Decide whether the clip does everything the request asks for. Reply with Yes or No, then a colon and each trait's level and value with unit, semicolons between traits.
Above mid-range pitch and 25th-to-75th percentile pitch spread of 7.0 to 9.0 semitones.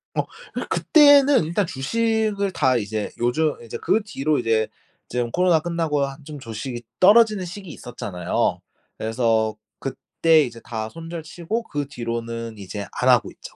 No: medium, 145 Hz; wide, 7.7 semitones